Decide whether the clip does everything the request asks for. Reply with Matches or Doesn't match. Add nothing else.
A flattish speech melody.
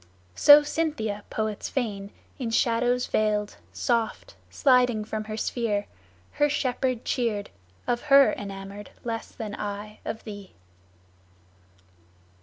Doesn't match